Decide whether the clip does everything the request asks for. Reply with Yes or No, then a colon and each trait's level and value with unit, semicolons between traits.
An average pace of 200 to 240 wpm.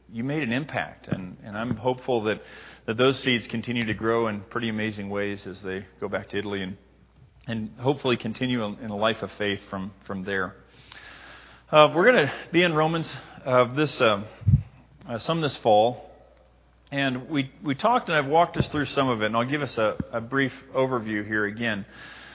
Yes: fast, 205 wpm